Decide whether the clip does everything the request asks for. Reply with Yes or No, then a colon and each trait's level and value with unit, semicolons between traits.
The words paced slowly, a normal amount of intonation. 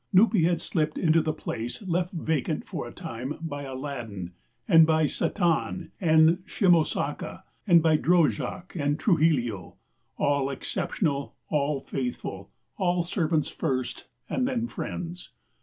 Yes: slow, 125 wpm; average, 3.9 semitones